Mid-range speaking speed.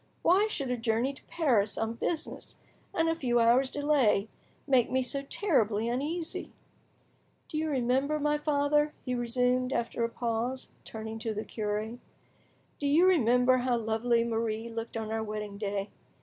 Yes: average, 160 wpm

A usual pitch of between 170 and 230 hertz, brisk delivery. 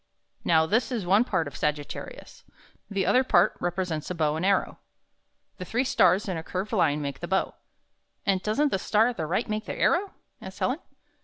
Yes: high, 190 Hz; fast, 220 wpm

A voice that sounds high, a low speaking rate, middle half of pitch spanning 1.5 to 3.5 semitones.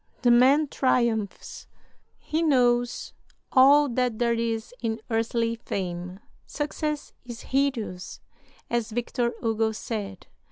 Yes: high, 235 Hz; slow, 110 wpm; narrow, 2.5 semitones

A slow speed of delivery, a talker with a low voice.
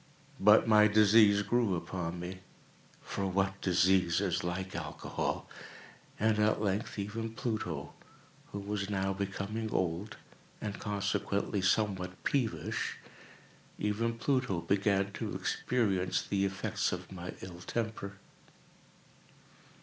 Yes: slow, 105 wpm; low, 100 Hz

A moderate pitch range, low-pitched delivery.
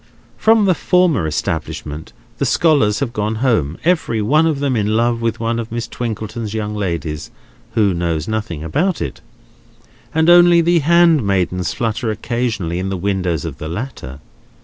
No: wide, 7.4 semitones; low, 110 Hz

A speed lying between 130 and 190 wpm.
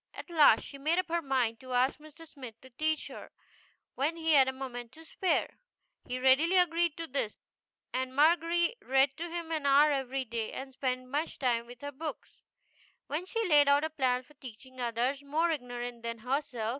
No: average, 200 wpm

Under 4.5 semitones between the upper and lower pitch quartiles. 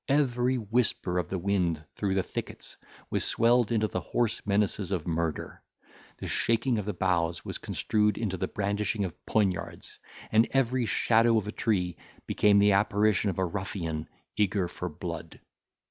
Yes: average, 3.6 semitones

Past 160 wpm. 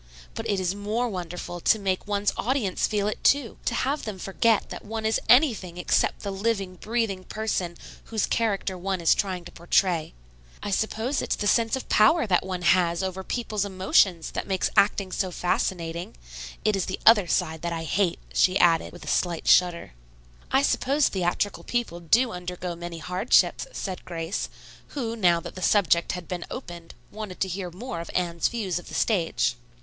Yes: average, 185 wpm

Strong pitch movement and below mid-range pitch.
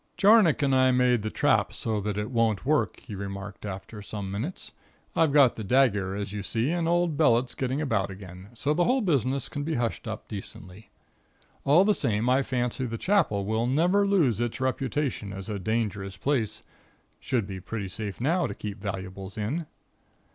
Yes: wide, 5.8 semitones; low, 115 Hz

